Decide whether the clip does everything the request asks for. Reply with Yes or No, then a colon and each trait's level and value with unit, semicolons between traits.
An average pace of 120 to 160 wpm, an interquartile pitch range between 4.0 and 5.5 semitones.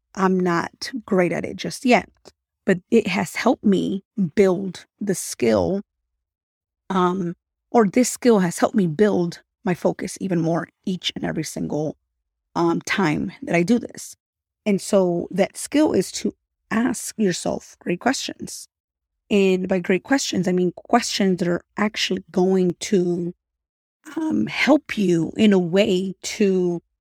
No: average, 145 wpm; average, 3.4 semitones